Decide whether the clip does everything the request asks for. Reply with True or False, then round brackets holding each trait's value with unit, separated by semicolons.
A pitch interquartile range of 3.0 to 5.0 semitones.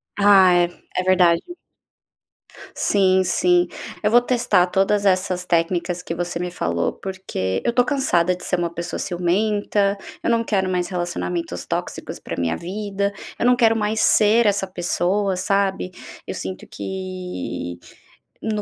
False (2.6 semitones)